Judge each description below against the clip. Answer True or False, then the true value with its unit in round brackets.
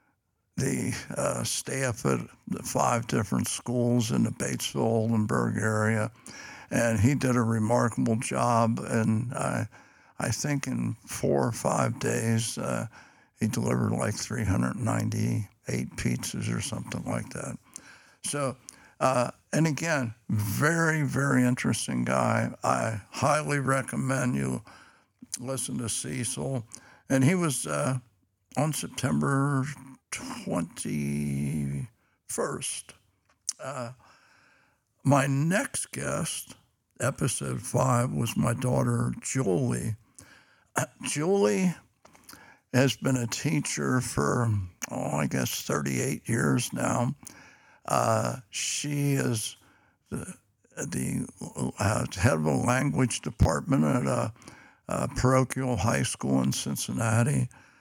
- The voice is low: True (120 Hz)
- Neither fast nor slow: False (105 wpm)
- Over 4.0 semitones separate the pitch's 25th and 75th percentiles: False (3.6 semitones)